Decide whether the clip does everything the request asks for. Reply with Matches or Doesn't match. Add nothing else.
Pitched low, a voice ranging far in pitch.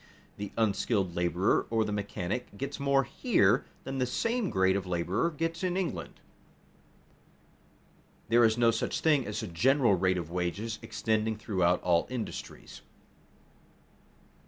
Matches